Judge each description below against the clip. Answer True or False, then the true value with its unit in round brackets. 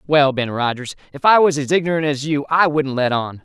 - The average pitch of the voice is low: False (145 Hz)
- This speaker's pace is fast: True (245 wpm)